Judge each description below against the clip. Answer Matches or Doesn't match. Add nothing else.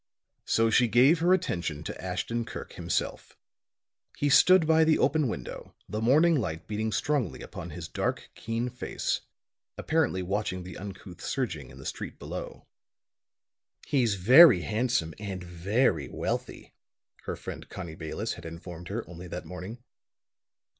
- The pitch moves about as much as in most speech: Doesn't match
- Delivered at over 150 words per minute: Doesn't match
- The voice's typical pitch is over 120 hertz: Doesn't match